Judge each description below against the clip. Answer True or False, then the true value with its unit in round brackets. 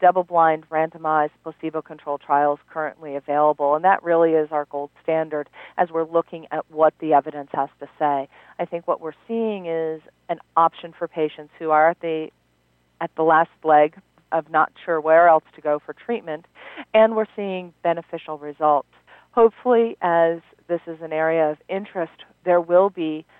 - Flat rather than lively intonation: True (2.1 semitones)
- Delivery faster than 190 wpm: False (175 wpm)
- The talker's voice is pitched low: False (160 Hz)